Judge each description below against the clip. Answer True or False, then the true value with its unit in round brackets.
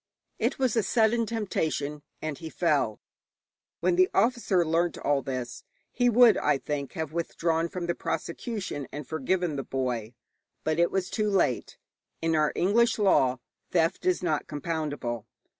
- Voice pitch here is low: False (165 Hz)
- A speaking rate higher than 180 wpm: False (155 wpm)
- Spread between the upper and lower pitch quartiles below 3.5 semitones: False (4.8 semitones)